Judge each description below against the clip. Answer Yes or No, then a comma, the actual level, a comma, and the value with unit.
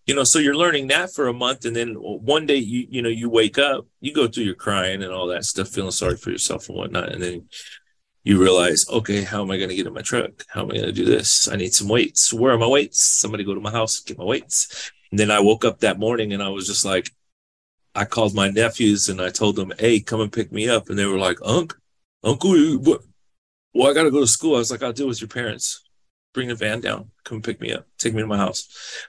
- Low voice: Yes, low, 110 Hz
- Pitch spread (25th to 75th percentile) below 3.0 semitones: No, average, 3.6 semitones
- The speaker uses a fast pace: Yes, fast, 270 wpm